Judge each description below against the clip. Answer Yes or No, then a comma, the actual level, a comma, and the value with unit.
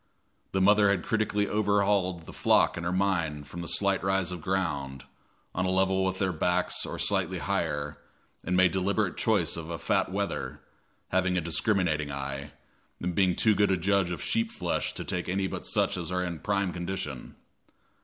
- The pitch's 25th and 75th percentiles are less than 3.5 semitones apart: Yes, average, 2.8 semitones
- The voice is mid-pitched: No, very low, 90 Hz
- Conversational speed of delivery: Yes, average, 185 wpm